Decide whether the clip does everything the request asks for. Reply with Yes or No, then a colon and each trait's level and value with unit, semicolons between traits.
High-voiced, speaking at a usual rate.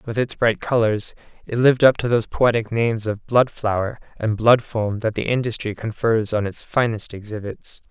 No: low, 110 Hz; average, 190 wpm